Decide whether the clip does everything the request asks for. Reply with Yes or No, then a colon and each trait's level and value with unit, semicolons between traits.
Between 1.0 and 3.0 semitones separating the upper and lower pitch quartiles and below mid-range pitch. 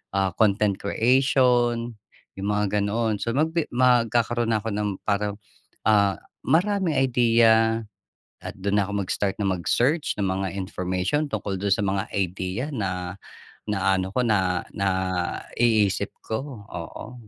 No: average, 3.7 semitones; low, 105 Hz